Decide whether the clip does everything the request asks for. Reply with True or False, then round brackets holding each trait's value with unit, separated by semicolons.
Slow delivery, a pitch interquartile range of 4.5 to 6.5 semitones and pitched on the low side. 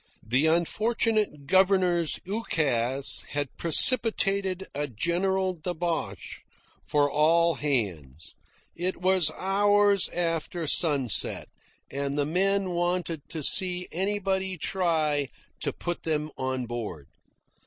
False (100 wpm; 4.8 semitones; 170 Hz)